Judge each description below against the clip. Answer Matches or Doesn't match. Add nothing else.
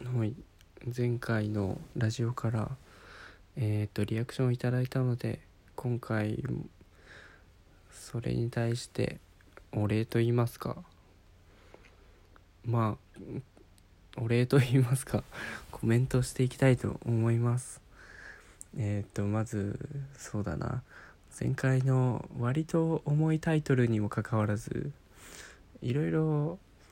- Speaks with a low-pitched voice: Matches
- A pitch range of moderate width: Matches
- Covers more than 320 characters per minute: Doesn't match